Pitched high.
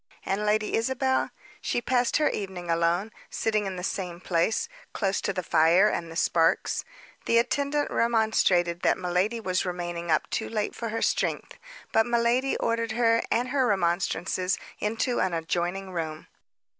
Yes: high, 200 Hz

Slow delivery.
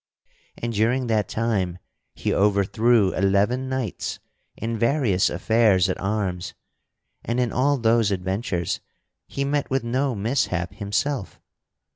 Yes: slow, 120 wpm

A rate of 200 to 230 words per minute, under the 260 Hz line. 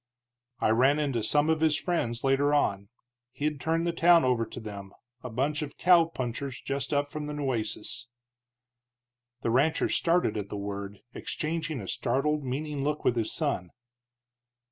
No: average, 160 wpm; medium, 140 Hz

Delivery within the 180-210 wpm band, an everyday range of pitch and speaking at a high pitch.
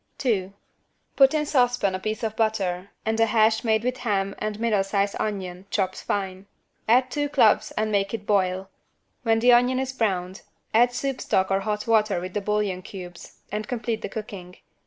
Yes: average, 185 wpm; average, 3.1 semitones; high, 215 Hz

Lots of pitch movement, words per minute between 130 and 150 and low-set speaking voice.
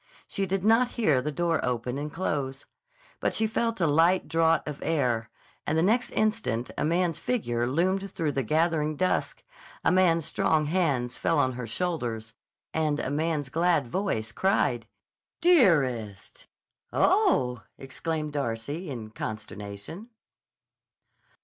No: wide, 6.5 semitones; slow, 135 wpm; medium, 155 Hz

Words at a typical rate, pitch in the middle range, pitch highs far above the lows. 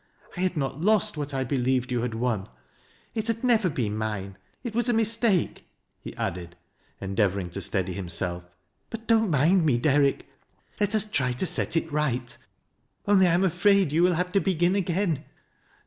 Yes: average, 180 wpm; medium, 150 Hz; wide, 8.6 semitones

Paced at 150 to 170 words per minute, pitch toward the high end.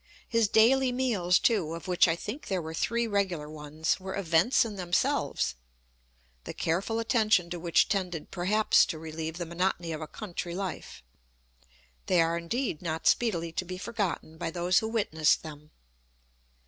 No: average, 160 wpm; medium, 180 Hz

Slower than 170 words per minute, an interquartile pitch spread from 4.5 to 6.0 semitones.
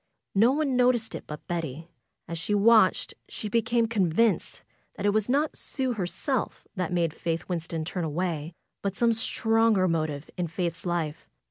Yes: average, 160 wpm; wide, 5.4 semitones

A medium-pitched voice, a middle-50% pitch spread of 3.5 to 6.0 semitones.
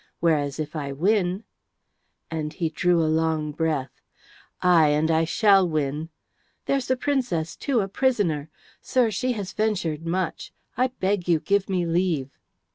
Yes: medium, 170 Hz; average, 4.4 semitones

